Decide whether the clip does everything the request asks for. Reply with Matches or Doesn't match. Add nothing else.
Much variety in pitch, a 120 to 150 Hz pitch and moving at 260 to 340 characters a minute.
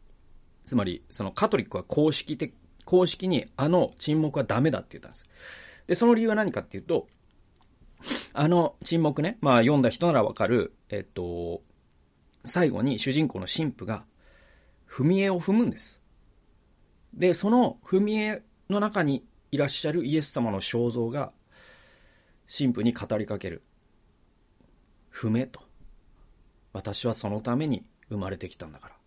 Matches